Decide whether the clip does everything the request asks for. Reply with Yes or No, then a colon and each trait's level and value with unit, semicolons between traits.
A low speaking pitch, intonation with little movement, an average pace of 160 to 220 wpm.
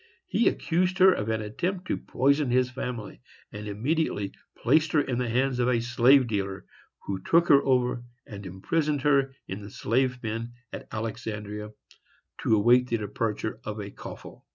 No: low, 120 Hz; average, 4.5 semitones; average, 170 wpm